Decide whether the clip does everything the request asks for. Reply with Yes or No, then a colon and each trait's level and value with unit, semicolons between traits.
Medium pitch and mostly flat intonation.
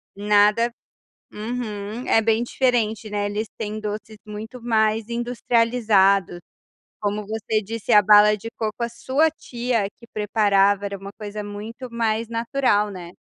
No: high, 215 Hz; narrow, 2.0 semitones